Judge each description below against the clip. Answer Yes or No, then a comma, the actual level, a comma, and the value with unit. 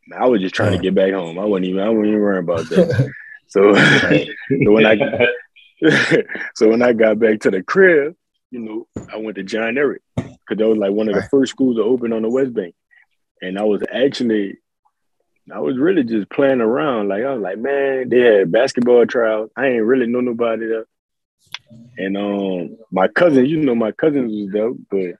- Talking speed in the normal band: No, fast, 210 wpm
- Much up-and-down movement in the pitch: No, average, 4.0 semitones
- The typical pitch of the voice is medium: No, low, 110 Hz